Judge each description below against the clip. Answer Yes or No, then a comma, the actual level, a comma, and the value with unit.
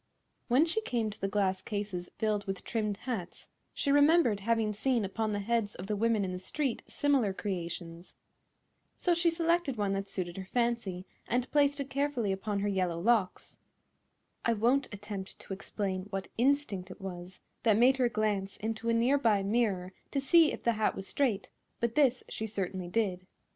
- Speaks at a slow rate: No, average, 185 wpm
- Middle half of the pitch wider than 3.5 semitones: Yes, average, 4.3 semitones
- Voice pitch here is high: Yes, high, 215 Hz